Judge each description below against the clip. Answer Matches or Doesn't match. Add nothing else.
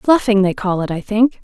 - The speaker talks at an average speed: Doesn't match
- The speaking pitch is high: Matches